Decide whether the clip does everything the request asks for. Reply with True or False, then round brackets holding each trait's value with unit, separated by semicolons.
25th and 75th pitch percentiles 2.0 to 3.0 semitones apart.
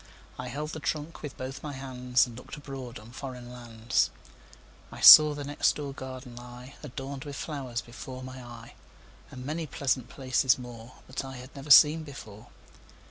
True (2.5 semitones)